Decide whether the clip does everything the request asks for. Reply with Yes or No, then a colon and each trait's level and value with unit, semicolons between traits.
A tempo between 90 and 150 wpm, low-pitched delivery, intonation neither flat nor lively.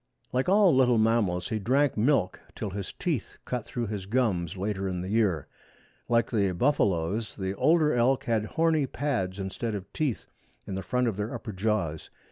No: average, 180 wpm; low, 110 Hz; average, 4.8 semitones